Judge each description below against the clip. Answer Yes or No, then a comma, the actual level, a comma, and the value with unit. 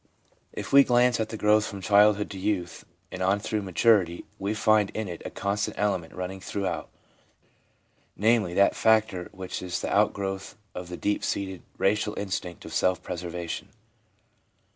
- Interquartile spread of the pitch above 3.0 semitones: No, average, 2.7 semitones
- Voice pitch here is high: No, low, 100 Hz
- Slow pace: No, average, 160 wpm